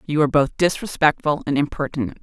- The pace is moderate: Yes, average, 160 wpm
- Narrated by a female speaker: Yes, female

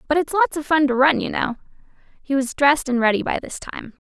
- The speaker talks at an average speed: No, fast, 250 wpm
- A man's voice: No, female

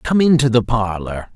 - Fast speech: No, average, 175 wpm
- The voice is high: No, low, 120 Hz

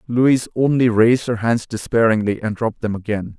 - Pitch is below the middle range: Yes, low, 115 Hz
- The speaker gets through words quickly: No, average, 175 wpm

